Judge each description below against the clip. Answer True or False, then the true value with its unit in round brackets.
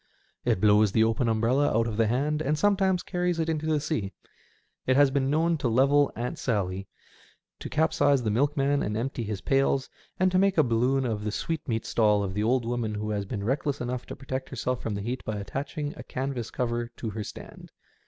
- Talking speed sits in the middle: False (210 wpm)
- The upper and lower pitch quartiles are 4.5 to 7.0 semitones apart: True (4.8 semitones)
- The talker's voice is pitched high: False (125 Hz)